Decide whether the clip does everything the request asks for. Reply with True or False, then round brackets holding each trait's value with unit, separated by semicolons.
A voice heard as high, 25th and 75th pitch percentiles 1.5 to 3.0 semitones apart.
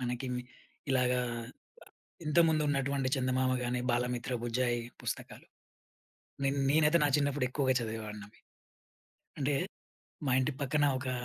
False (130 Hz; 2.5 semitones)